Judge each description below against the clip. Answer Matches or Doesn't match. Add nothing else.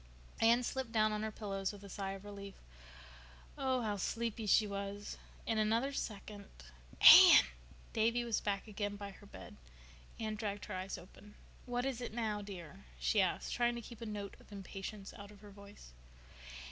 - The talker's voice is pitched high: Matches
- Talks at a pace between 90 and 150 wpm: Doesn't match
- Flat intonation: Matches